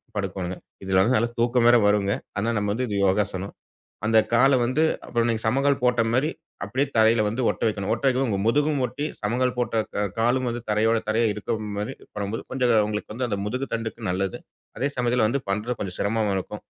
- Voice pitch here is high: No, low, 115 Hz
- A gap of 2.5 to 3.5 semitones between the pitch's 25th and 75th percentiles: Yes, average, 3.2 semitones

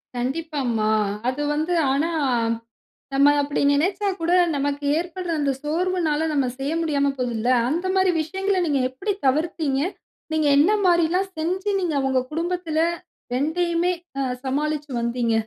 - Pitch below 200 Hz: No, very high, 310 Hz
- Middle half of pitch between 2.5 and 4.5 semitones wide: Yes, average, 4.0 semitones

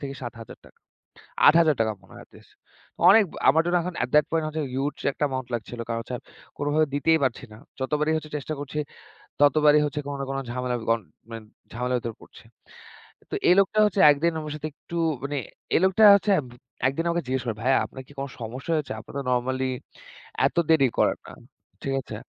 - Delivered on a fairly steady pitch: No, average, 3.7 semitones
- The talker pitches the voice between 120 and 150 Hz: Yes, medium, 140 Hz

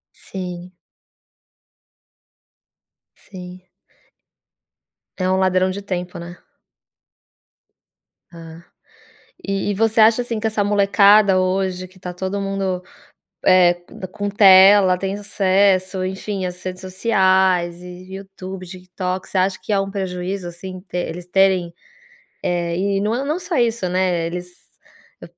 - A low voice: No, medium, 185 Hz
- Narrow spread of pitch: Yes, narrow, 1.6 semitones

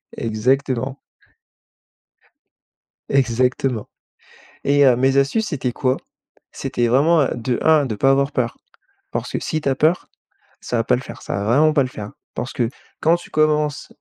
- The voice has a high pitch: No, low, 135 Hz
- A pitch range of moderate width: Yes, average, 3.2 semitones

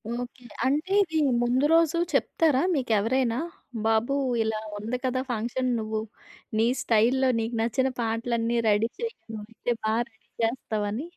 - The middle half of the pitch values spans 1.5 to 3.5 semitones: Yes, average, 2.9 semitones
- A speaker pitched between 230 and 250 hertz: Yes, high, 235 Hz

